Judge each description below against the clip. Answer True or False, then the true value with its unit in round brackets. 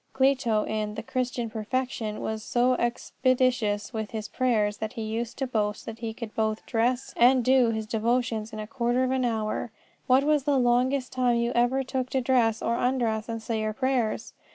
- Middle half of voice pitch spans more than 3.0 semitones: False (2.7 semitones)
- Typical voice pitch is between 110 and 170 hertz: False (235 Hz)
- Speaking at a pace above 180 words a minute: True (195 wpm)